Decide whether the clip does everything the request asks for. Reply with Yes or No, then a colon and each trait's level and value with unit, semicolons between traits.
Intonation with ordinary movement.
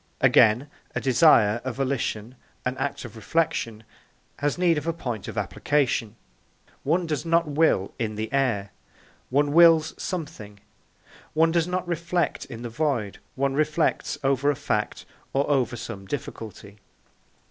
No: wide, 5.7 semitones